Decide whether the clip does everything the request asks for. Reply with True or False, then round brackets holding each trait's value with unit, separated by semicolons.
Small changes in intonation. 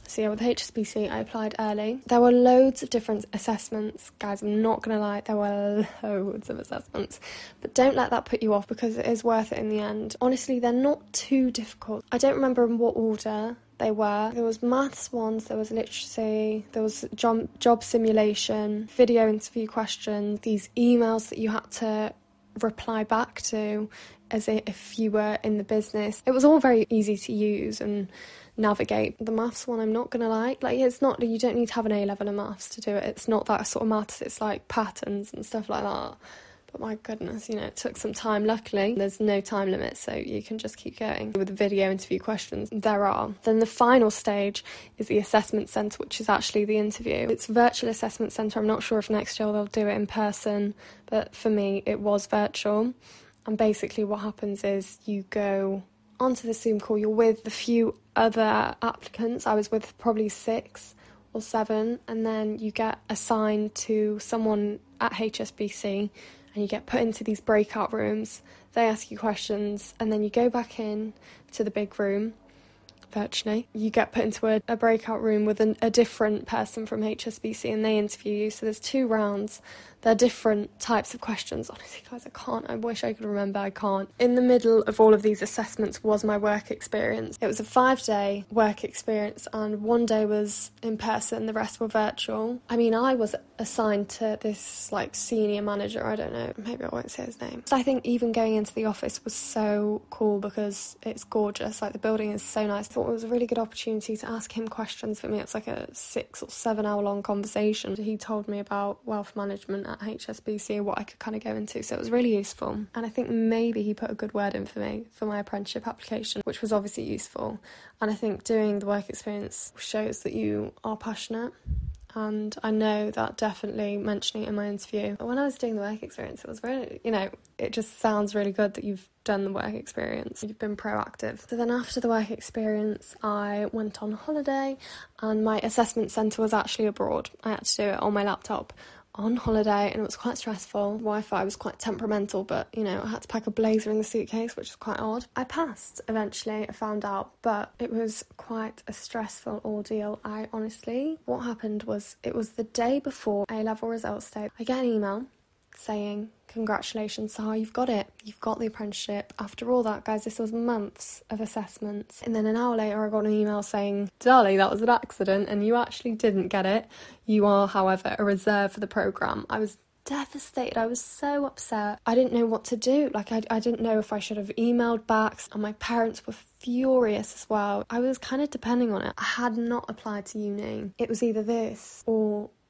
True (1.6 semitones)